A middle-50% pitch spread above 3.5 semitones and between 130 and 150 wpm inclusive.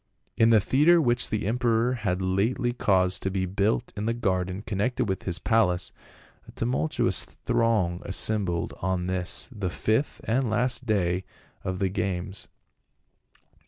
Yes: average, 3.9 semitones; average, 145 wpm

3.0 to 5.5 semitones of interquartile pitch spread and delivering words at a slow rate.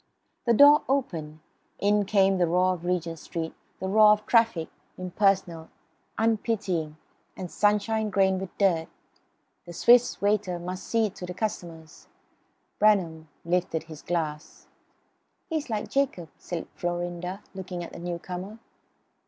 Yes: average, 3.6 semitones; slow, 130 wpm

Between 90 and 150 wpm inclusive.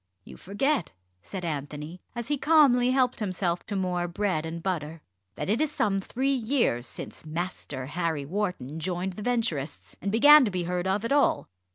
No: average, 180 wpm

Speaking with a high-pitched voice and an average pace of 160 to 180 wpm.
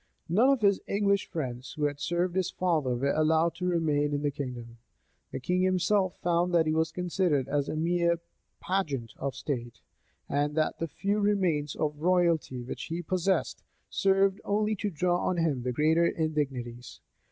No: medium, 165 Hz; average, 175 wpm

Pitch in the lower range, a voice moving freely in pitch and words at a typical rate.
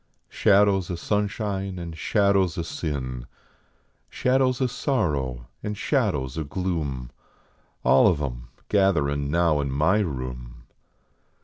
No: very low, 85 Hz; wide, 6.8 semitones; slow, 115 wpm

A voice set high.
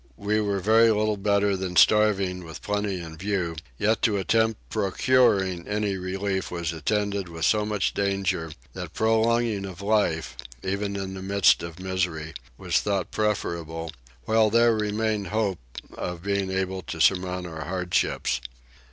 No: low, 100 Hz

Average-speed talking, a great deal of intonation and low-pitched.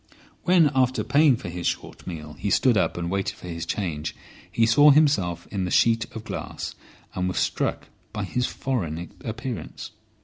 Yes: average, 175 wpm; wide, 6.7 semitones; low, 105 Hz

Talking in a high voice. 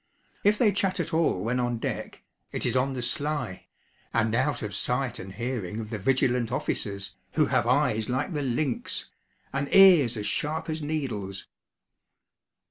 No: low, 125 Hz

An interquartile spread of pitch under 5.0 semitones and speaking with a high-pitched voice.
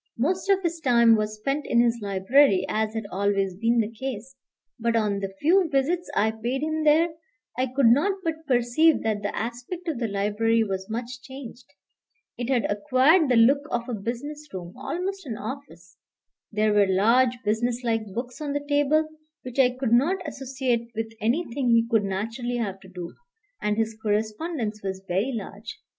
Yes: average, 4.6 semitones; high, 235 Hz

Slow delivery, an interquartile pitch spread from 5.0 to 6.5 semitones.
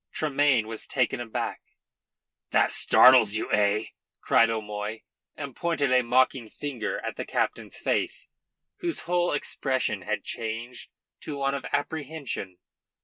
No: slow, 130 wpm; average, 4.5 semitones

